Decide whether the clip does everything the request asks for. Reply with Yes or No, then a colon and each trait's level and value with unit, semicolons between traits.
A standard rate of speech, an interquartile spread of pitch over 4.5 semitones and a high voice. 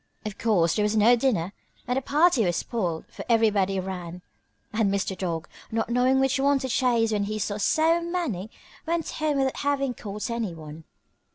Yes: average, 180 wpm; wide, 5.6 semitones; high, 225 Hz